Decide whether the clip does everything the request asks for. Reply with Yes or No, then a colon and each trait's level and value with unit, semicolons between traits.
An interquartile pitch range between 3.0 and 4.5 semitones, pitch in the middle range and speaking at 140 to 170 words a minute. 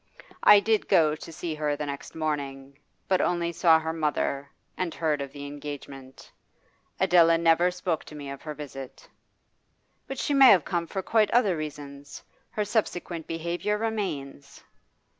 Yes: average, 3.9 semitones; medium, 160 Hz; average, 160 wpm